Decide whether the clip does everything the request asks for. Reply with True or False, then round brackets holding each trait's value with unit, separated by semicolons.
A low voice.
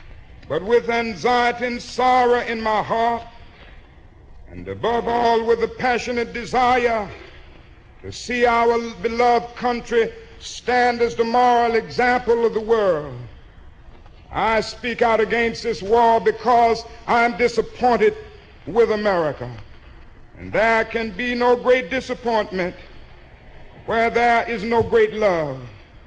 False (230 Hz)